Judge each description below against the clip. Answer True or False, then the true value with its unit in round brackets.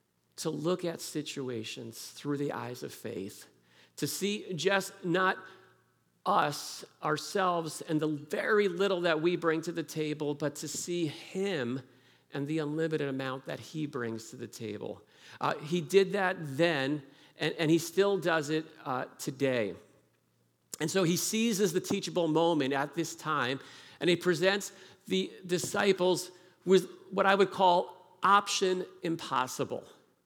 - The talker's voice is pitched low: False (165 Hz)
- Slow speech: False (145 wpm)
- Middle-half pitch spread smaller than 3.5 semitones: False (4.3 semitones)